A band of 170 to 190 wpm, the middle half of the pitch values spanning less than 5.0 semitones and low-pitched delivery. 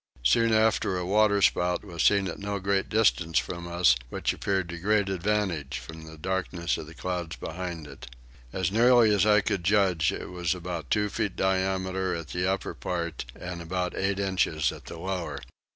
Yes: average, 185 wpm; average, 2.7 semitones; very low, 90 Hz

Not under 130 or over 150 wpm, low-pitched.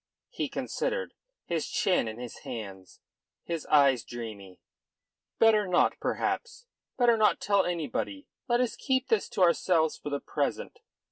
No: average, 140 wpm; medium, 175 Hz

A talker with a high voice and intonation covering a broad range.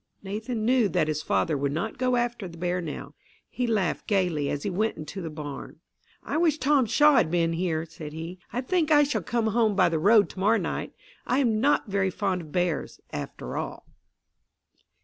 Yes: high, 195 Hz; wide, 6.4 semitones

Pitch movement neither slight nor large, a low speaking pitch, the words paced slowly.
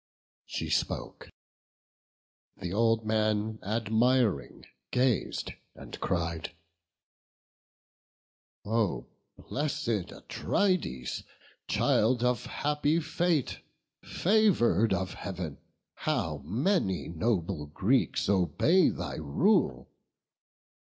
No: wide, 7.3 semitones; low, 110 Hz; slow, 75 wpm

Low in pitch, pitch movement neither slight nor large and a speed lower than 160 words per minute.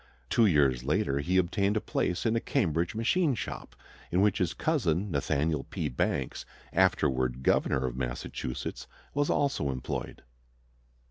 No: very low, 85 Hz; wide, 7.9 semitones; average, 140 wpm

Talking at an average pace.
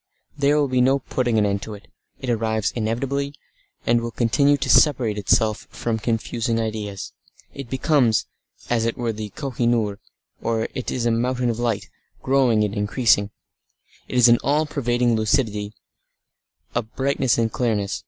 Yes: average, 170 wpm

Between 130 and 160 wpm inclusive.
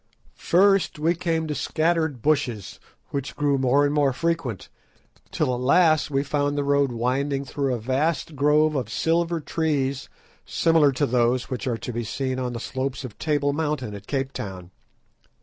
No: average, 170 wpm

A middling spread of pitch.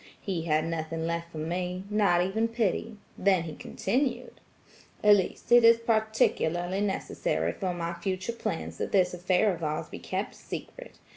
Yes: average, 4.1 semitones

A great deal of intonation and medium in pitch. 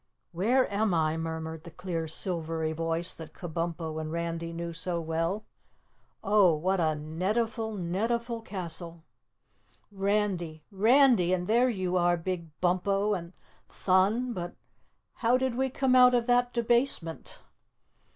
No: average, 5.0 semitones; medium, 180 Hz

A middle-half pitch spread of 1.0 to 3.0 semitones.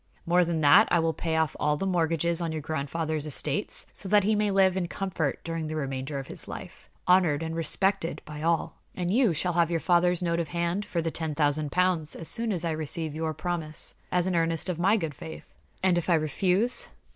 Yes: narrow, 2.4 semitones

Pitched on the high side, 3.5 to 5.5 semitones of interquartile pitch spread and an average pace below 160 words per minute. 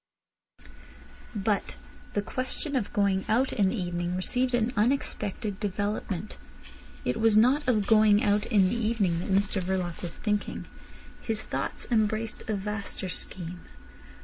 No: high, 210 Hz; average, 2.8 semitones; average, 140 wpm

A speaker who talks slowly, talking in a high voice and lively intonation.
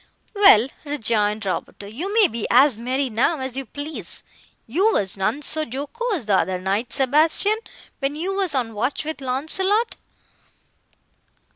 No: average, 145 wpm; very high, 270 Hz; wide, 6.3 semitones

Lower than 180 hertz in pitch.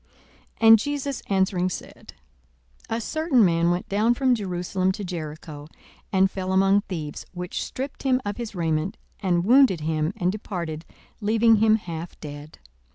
No: high, 190 Hz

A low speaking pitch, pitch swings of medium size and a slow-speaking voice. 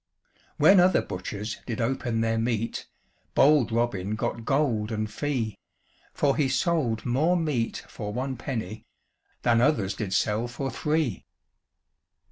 Yes: low, 120 Hz; average, 4.1 semitones; slow, 130 wpm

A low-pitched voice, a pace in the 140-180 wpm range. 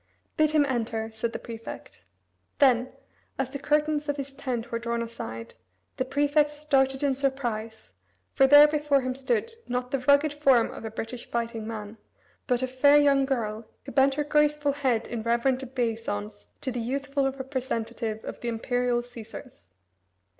No: very high, 260 Hz; average, 165 wpm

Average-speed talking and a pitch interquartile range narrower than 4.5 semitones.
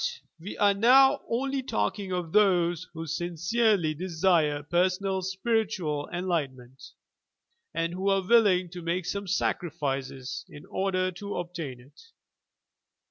No: slow, 125 wpm; average, 3.6 semitones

